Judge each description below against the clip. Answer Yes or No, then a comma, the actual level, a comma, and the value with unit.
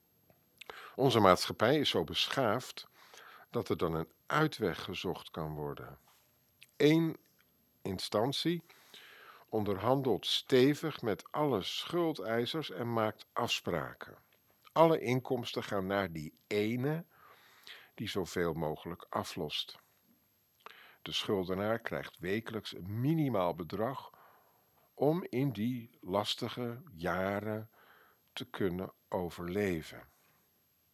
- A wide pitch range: Yes, wide, 7.0 semitones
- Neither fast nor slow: No, slow, 95 wpm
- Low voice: Yes, low, 115 Hz